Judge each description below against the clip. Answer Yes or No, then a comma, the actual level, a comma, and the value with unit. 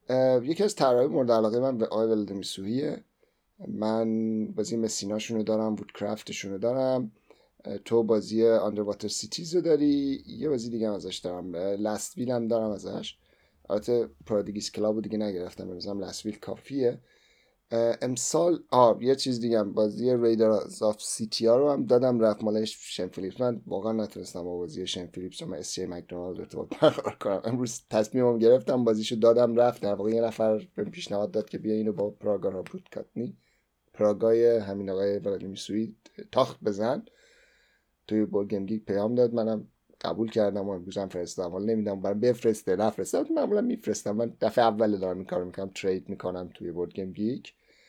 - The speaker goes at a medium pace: No, fast, 175 wpm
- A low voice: Yes, low, 110 Hz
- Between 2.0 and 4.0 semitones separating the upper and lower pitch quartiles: Yes, average, 2.7 semitones